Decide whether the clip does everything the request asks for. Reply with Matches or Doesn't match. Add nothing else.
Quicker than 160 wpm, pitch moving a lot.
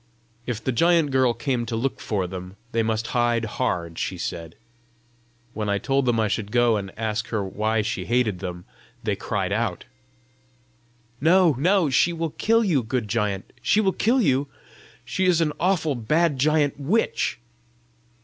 Matches